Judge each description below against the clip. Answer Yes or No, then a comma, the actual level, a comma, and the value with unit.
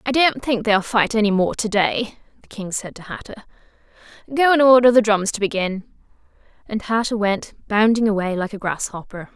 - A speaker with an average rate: Yes, average, 185 wpm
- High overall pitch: Yes, high, 215 Hz